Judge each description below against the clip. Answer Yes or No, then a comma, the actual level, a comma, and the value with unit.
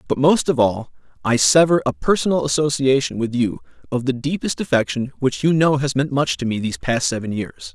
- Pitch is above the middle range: No, low, 135 Hz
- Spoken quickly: Yes, fast, 210 wpm